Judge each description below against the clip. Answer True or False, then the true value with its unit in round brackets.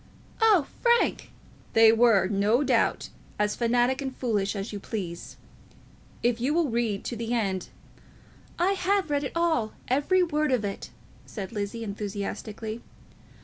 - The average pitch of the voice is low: False (235 Hz)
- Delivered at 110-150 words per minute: True (145 wpm)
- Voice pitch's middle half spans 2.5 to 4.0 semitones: False (5.6 semitones)